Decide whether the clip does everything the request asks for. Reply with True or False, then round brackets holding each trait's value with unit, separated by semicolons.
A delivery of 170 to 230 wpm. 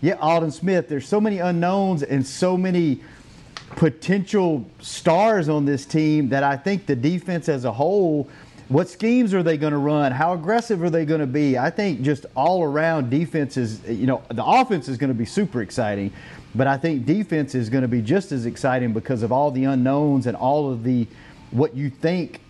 True (205 wpm)